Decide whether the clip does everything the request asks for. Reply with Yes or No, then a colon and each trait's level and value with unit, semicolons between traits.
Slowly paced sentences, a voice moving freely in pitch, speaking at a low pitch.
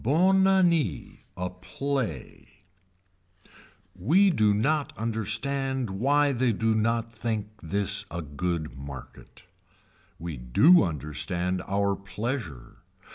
Yes: slow, 100 wpm; wide, 7.6 semitones; low, 110 Hz